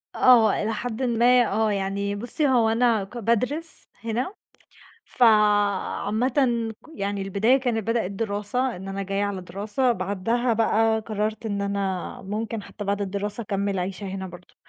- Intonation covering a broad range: No, average, 2.8 semitones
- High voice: Yes, high, 215 Hz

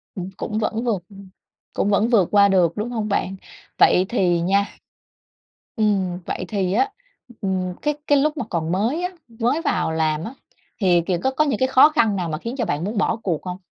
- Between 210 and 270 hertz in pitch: No, high, 200 Hz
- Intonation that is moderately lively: Yes, average, 4.6 semitones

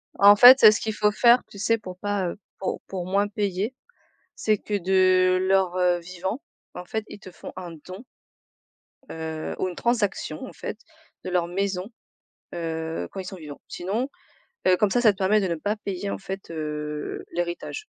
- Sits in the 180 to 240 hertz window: Yes, high, 190 Hz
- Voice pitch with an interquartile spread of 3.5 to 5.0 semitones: No, average, 2.7 semitones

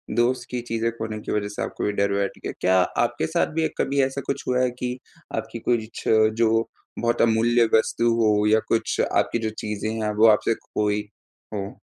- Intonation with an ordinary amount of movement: No, narrow, 1.9 semitones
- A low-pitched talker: Yes, low, 115 Hz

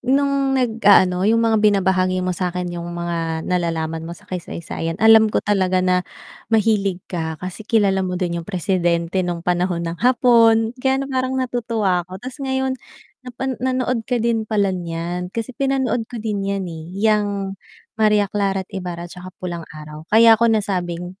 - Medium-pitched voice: No, high, 195 Hz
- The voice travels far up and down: No, average, 4.3 semitones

